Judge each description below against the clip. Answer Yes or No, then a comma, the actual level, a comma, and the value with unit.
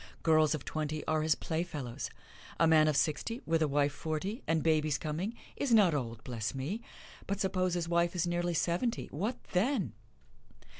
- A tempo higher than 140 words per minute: Yes, average, 170 wpm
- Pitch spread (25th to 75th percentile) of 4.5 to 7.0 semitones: No, average, 3.3 semitones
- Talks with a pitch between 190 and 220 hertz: No, medium, 160 Hz